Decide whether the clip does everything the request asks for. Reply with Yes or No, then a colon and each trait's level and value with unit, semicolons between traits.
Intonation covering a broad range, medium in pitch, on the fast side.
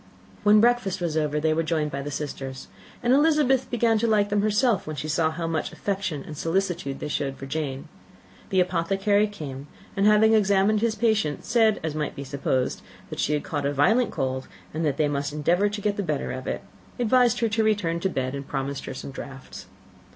Yes: wide, 6.5 semitones; medium, 170 Hz; fast, 210 wpm